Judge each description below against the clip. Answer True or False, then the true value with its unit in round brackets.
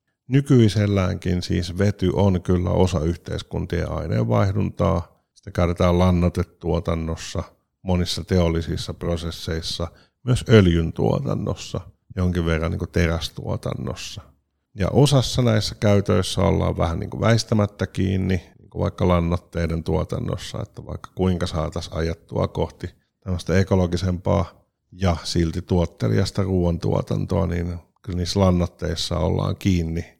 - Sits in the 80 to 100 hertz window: True (90 Hz)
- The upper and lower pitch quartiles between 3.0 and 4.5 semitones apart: False (2.6 semitones)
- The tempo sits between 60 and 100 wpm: True (95 wpm)